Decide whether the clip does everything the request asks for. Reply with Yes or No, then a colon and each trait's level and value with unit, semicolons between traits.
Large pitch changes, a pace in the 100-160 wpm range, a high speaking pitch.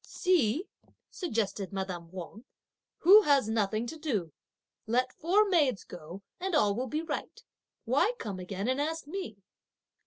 Yes: wide, 8.5 semitones; average, 145 wpm; high, 240 Hz